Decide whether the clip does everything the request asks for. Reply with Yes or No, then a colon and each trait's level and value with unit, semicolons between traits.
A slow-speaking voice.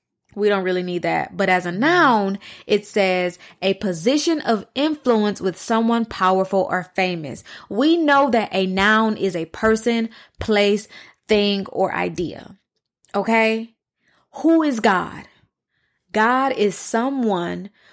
Yes: slow, 130 wpm